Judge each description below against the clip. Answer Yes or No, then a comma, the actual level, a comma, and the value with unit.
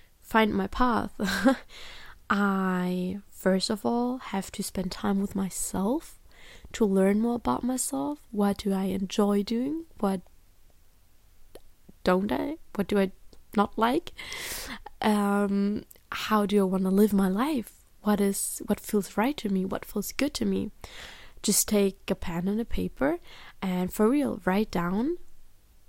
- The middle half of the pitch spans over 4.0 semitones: No, average, 3.5 semitones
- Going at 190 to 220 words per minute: No, average, 150 wpm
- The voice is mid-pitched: No, high, 205 Hz